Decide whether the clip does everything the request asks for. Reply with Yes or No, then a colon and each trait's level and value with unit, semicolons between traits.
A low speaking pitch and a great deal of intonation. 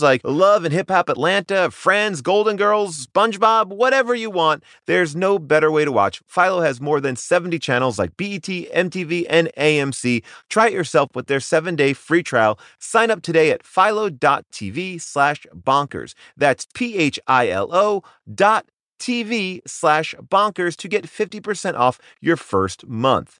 No: medium, 175 Hz; wide, 5.7 semitones